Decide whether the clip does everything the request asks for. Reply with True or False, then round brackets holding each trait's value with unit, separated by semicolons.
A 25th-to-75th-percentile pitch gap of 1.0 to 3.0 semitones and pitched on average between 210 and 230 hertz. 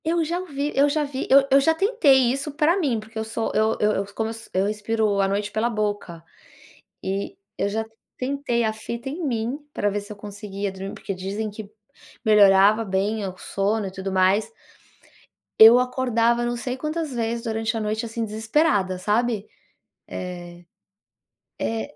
False (4.2 semitones; 220 Hz)